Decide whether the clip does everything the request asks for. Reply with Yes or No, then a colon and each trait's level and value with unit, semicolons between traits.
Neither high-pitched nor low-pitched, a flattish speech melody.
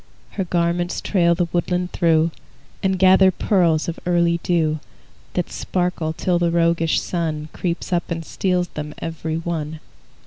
Yes: medium, 170 Hz; narrow, 1.6 semitones